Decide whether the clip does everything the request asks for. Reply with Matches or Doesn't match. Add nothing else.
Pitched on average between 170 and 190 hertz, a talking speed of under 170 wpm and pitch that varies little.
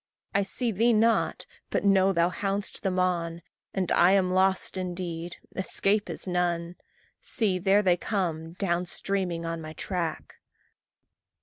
Matches